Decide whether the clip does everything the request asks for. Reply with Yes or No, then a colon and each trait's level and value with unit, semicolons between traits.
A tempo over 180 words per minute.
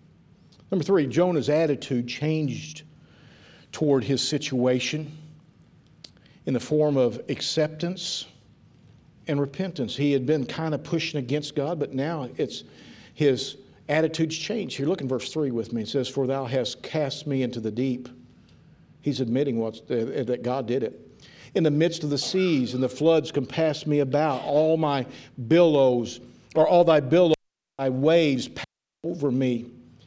No: average, 155 wpm